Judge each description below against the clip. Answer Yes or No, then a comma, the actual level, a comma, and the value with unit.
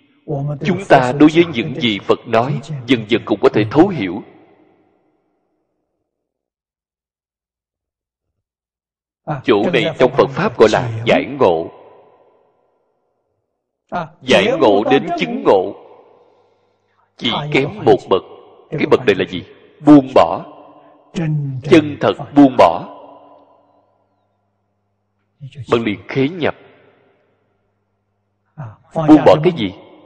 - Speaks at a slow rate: Yes, slow, 105 wpm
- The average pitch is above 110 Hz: Yes, medium, 140 Hz